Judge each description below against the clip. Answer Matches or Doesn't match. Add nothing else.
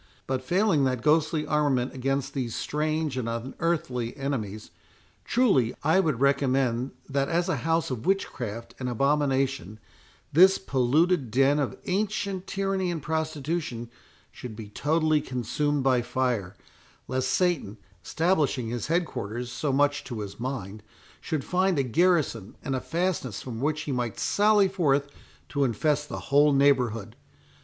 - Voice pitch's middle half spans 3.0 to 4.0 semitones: Doesn't match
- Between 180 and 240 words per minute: Doesn't match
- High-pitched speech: Doesn't match